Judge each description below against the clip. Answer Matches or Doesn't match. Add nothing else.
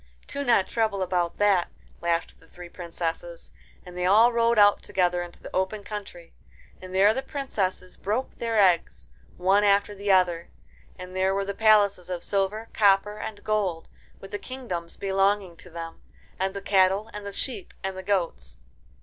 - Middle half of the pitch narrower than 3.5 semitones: Matches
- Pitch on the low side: Doesn't match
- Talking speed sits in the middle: Matches